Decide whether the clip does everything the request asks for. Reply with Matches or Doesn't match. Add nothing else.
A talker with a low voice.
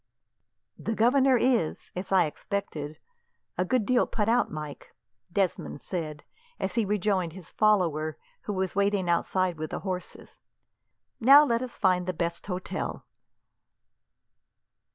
Doesn't match